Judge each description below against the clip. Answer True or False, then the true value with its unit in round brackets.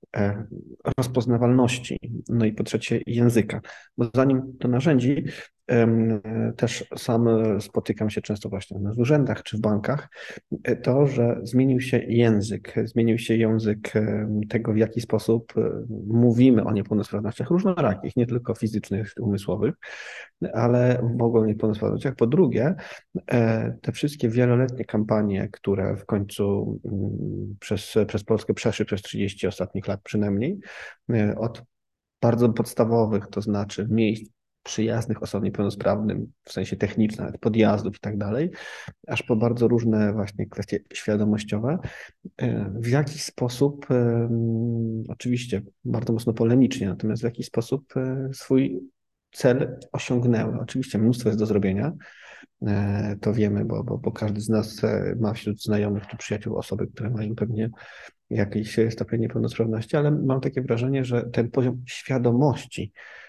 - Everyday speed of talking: True (125 wpm)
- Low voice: True (115 Hz)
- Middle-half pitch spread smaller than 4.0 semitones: True (2.6 semitones)